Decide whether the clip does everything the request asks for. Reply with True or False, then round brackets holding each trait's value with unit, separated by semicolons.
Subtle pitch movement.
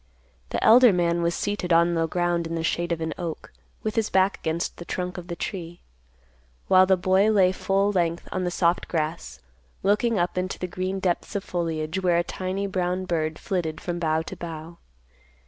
True (2.0 semitones)